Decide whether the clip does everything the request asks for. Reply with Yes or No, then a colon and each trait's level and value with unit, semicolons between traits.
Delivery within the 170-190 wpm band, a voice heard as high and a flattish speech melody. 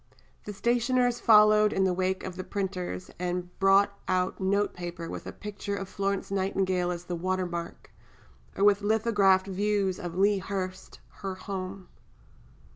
No: average, 155 wpm; high, 195 Hz; narrow, 1.7 semitones